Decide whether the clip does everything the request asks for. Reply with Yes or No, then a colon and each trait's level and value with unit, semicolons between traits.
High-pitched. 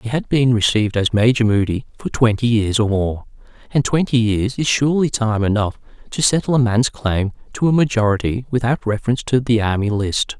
No: low, 115 Hz